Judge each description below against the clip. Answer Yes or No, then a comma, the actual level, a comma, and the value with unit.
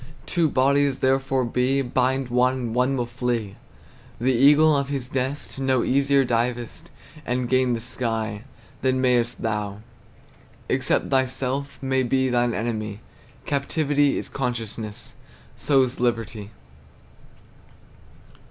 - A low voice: Yes, low, 125 Hz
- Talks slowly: Yes, slow, 115 wpm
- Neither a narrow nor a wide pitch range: No, narrow, 2.2 semitones